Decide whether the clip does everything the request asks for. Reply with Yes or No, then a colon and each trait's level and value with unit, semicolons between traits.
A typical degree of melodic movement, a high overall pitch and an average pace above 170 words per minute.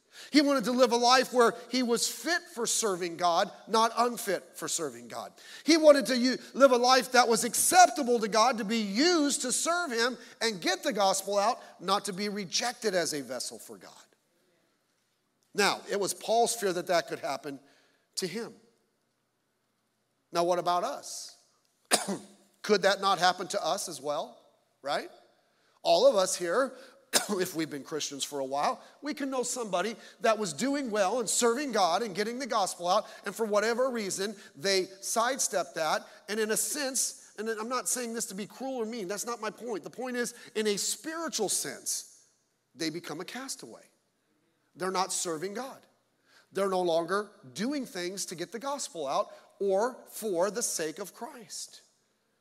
Yes: average, 4.9 semitones; high, 220 Hz; average, 180 wpm